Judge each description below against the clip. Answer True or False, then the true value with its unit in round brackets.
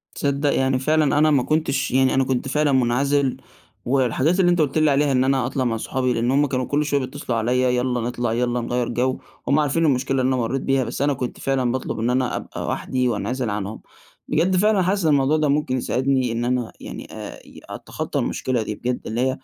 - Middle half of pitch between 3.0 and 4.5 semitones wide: False (2.5 semitones)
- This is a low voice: True (130 Hz)